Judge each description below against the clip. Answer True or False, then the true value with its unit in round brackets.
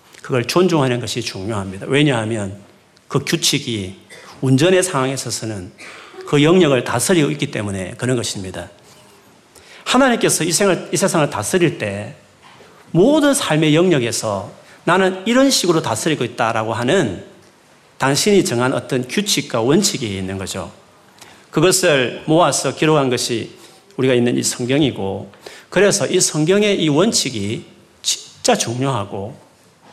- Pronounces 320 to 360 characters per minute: False (285 characters per minute)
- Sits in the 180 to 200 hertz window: False (135 Hz)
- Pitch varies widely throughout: True (7.8 semitones)